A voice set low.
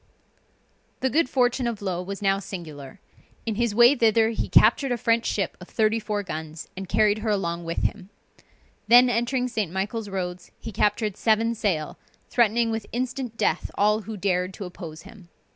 No: high, 210 Hz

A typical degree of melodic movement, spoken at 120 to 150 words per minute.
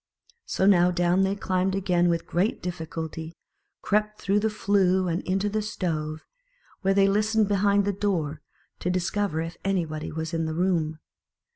No: average, 3.3 semitones; average, 160 wpm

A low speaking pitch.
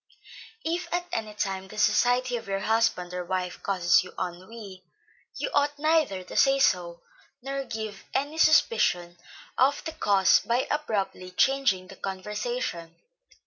No: high, 215 Hz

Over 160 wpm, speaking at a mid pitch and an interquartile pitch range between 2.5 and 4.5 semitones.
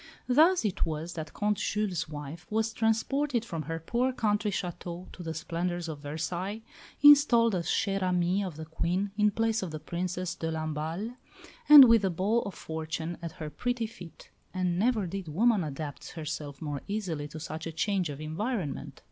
No: average, 180 wpm; medium, 180 Hz; average, 5.2 semitones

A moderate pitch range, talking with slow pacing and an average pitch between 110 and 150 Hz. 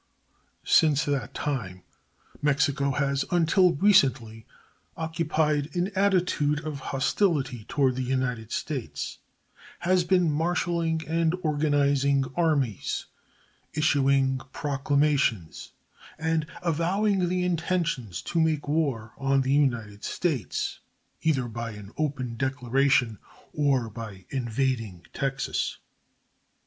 Yes: average, 4.0 semitones; slow, 100 wpm; medium, 140 Hz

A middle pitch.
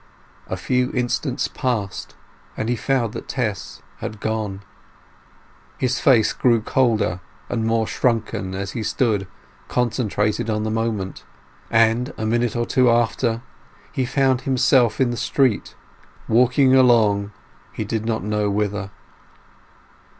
No: low, 115 Hz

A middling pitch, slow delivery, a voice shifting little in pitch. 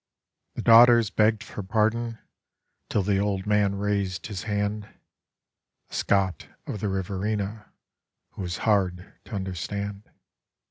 No: low, 100 Hz; slow, 125 wpm; narrow, 1.8 semitones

